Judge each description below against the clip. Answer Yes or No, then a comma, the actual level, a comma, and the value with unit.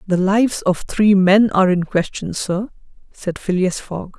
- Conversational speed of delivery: Yes, average, 170 wpm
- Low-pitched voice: No, high, 190 Hz